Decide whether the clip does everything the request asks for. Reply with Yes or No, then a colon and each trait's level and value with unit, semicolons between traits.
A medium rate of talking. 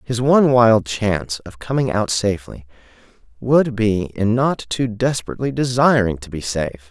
Yes: average, 155 wpm